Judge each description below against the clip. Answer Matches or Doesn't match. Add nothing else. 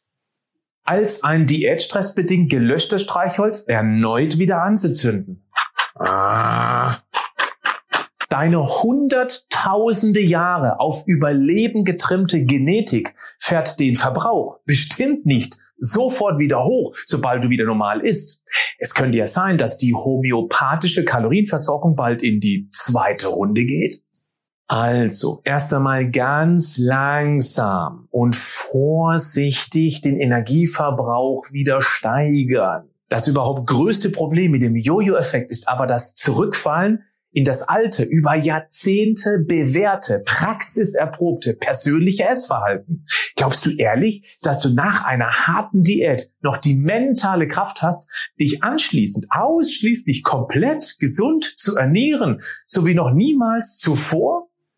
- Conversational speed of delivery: Doesn't match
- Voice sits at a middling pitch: Matches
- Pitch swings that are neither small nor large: Doesn't match